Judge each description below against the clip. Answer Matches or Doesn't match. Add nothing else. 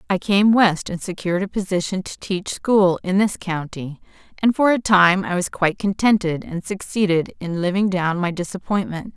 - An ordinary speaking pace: Matches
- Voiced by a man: Doesn't match